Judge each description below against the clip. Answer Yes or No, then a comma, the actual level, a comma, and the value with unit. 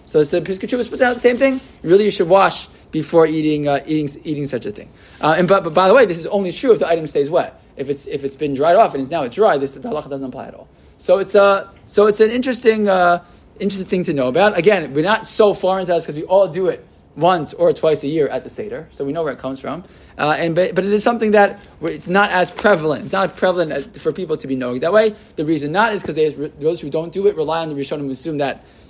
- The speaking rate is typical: No, fast, 280 wpm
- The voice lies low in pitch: No, medium, 175 Hz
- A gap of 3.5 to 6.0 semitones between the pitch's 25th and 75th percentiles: Yes, average, 5.0 semitones